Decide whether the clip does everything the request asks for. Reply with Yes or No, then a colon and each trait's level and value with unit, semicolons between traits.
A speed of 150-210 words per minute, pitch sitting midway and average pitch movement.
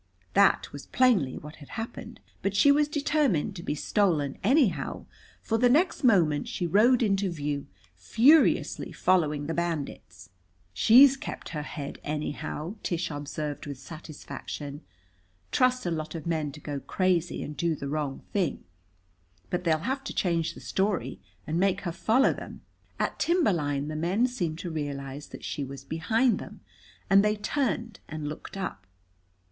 No: average, 160 wpm; medium, 170 Hz; wide, 6.7 semitones